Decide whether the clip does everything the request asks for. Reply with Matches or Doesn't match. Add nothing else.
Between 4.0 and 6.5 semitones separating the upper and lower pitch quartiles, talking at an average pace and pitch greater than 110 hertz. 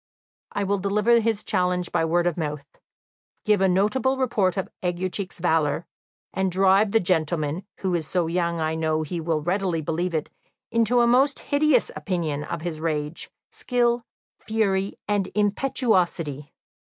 Matches